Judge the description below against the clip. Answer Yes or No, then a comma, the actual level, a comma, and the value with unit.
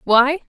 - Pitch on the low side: No, very high, 270 Hz